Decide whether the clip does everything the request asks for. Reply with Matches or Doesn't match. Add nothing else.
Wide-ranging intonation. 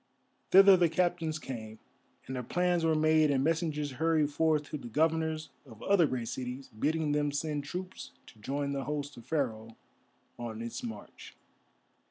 Doesn't match